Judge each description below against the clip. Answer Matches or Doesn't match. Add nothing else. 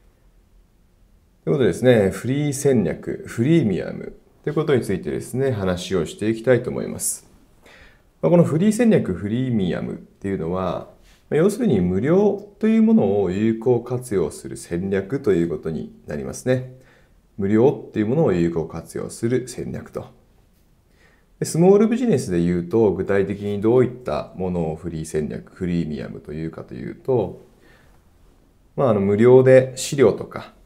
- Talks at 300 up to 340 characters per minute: Matches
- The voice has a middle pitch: Doesn't match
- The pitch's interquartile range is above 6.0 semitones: Matches